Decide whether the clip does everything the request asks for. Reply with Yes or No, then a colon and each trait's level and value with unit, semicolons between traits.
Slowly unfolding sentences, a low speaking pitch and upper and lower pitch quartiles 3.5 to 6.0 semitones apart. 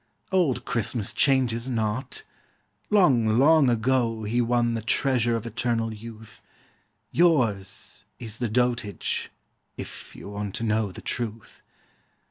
No: slow, 120 wpm; low, 115 Hz; narrow, 2.4 semitones